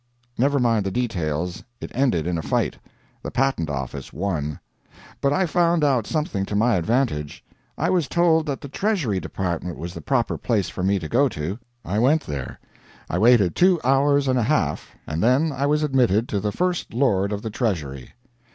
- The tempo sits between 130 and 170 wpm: No, average, 190 wpm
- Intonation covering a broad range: Yes, wide, 7.7 semitones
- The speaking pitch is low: Yes, low, 115 Hz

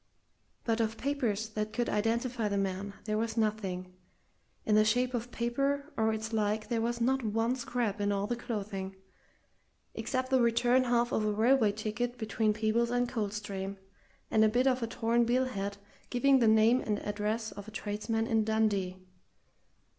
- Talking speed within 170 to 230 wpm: Yes, average, 175 wpm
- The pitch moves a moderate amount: No, narrow, 2.3 semitones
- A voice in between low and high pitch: No, high, 220 Hz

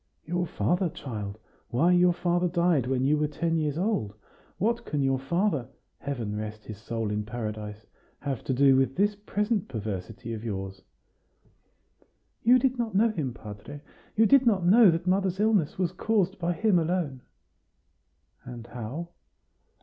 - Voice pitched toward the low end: No, medium, 155 Hz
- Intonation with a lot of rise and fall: Yes, wide, 8.0 semitones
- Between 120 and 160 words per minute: Yes, average, 155 wpm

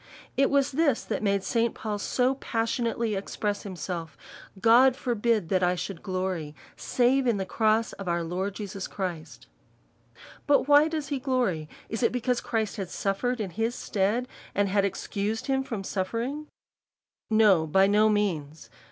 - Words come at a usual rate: Yes, average, 160 wpm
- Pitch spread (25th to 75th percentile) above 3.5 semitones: Yes, average, 4.4 semitones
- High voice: Yes, high, 215 Hz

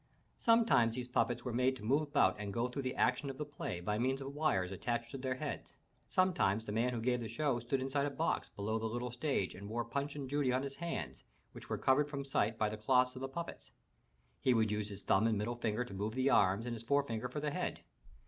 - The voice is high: No, low, 125 Hz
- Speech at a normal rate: No, fast, 250 wpm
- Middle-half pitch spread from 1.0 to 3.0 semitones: No, average, 3.7 semitones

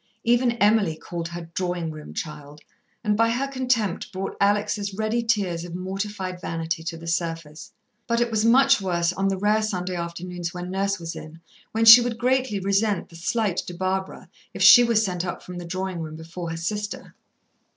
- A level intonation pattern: No, average, 4.2 semitones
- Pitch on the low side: No, high, 190 Hz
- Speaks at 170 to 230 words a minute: Yes, average, 190 wpm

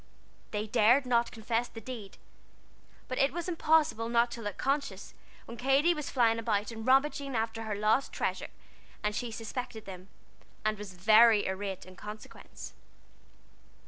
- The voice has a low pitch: No, high, 225 Hz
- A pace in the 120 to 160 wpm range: Yes, average, 150 wpm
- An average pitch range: Yes, average, 3.5 semitones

